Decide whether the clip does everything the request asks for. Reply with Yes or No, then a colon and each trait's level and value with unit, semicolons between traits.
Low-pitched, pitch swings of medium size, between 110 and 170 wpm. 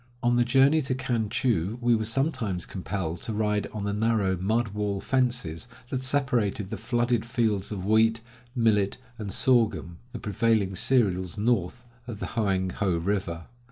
Yes: low, 110 Hz; average, 3.8 semitones; average, 160 wpm